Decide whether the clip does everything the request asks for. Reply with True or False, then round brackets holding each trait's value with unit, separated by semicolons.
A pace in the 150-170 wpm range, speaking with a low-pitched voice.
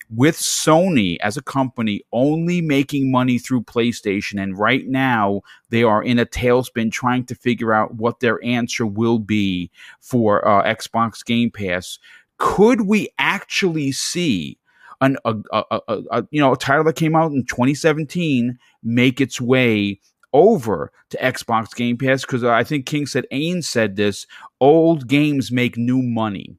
True (160 wpm; 125 Hz)